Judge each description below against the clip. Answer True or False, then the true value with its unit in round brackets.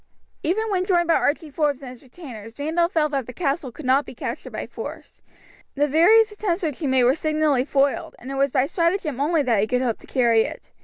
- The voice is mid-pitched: False (285 Hz)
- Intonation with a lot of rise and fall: False (4.7 semitones)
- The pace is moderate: False (235 wpm)